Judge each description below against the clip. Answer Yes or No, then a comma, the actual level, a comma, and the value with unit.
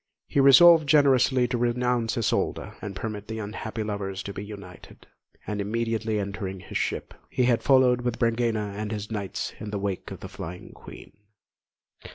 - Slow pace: No, average, 170 wpm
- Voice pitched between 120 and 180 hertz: No, low, 110 Hz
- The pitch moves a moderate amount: Yes, average, 3.3 semitones